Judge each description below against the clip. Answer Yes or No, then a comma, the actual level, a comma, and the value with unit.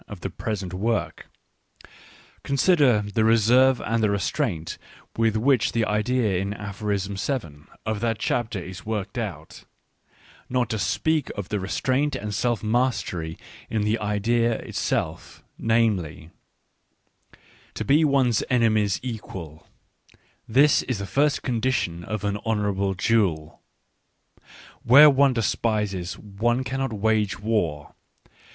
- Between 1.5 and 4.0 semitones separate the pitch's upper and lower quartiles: Yes, average, 3.4 semitones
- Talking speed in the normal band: No, slow, 130 wpm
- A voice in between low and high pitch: No, low, 110 Hz